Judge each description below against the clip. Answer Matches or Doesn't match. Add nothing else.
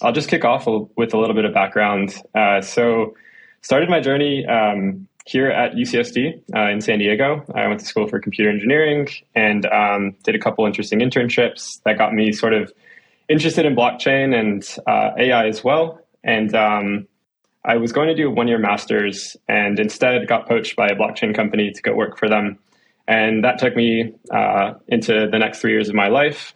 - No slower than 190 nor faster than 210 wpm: Matches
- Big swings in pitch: Doesn't match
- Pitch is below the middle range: Matches